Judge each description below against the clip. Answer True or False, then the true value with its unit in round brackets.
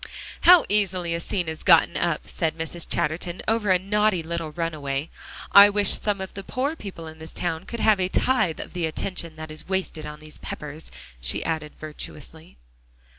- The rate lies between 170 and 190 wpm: True (185 wpm)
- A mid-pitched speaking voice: True (170 Hz)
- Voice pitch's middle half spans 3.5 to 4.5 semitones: True (3.9 semitones)